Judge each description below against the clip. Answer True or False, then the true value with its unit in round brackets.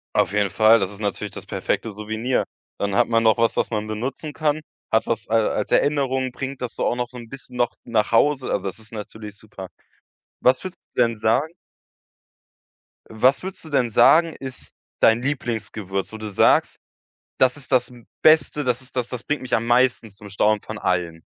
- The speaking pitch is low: True (115 Hz)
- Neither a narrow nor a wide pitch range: True (3.4 semitones)